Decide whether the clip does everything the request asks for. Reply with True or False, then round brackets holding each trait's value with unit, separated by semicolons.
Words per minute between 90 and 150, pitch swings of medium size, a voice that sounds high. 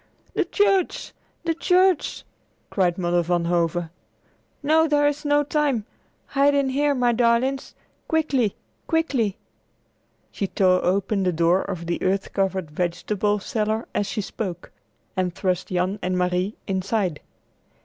False (135 wpm; 7.6 semitones; 205 Hz)